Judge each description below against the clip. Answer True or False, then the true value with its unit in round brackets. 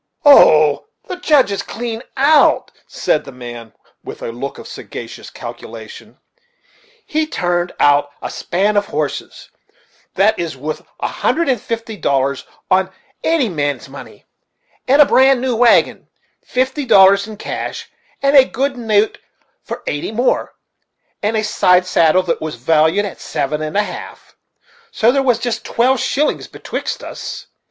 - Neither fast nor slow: True (150 wpm)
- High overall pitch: True (205 Hz)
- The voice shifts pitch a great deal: True (8.6 semitones)